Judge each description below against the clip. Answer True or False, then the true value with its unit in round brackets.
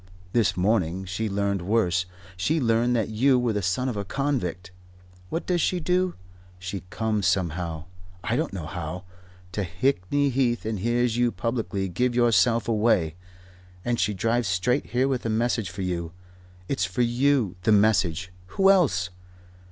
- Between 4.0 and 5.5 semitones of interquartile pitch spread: True (5.1 semitones)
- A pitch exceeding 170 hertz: False (110 Hz)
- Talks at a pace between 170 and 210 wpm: False (160 wpm)